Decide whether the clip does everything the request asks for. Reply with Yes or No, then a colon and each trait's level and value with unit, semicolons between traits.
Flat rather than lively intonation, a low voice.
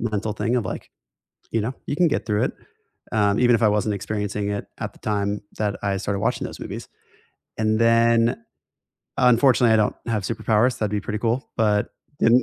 Yes: narrow, 2.1 semitones; low, 110 Hz